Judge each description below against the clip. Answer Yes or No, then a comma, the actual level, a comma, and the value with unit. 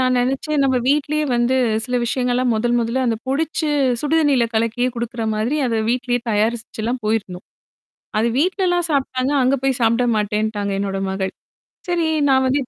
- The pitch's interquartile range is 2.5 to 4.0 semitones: Yes, average, 3.4 semitones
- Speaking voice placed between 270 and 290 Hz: No, high, 245 Hz